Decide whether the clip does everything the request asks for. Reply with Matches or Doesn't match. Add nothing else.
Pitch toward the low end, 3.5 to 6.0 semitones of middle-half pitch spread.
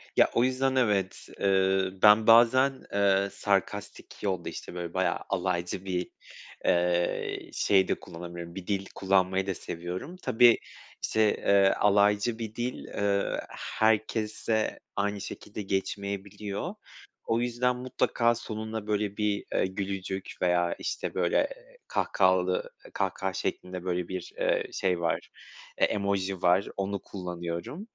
Doesn't match